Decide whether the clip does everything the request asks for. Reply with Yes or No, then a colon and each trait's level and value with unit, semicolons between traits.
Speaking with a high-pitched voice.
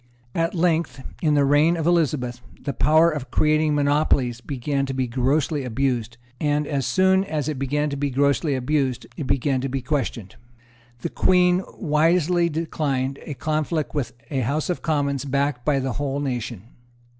No: medium, 145 Hz